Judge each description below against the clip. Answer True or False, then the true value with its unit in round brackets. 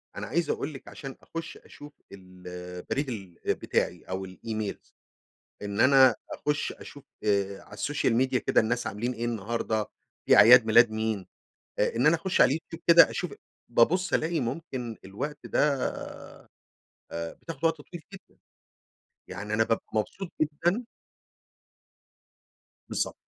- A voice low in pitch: True (120 Hz)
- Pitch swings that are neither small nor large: False (6.3 semitones)